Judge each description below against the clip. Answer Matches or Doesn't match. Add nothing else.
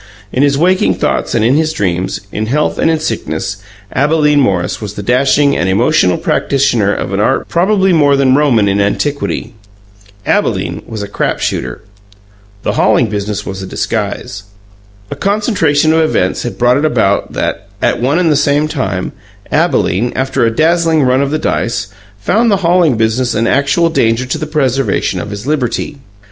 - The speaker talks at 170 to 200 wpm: Matches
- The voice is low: Matches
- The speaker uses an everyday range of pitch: Doesn't match